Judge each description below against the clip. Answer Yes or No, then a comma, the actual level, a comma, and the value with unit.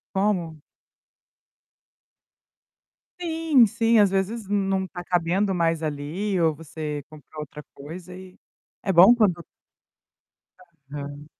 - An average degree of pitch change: Yes, average, 4.5 semitones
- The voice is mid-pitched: Yes, medium, 180 Hz